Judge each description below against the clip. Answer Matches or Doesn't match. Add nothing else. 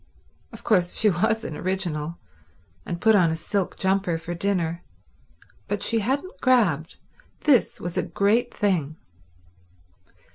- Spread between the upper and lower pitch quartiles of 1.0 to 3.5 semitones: Doesn't match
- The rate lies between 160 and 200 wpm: Doesn't match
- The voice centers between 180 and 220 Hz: Matches